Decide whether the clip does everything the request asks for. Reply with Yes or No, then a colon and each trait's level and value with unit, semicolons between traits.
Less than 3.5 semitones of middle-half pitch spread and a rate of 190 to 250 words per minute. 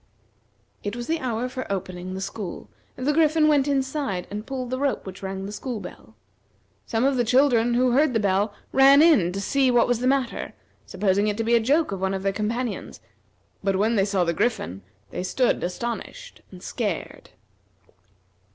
No: average, 5.3 semitones; average, 195 wpm